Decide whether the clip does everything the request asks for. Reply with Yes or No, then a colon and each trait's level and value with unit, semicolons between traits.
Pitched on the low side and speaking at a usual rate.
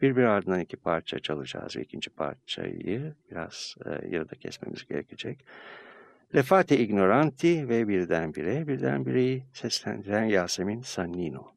Yes: low, 120 Hz; average, 120 wpm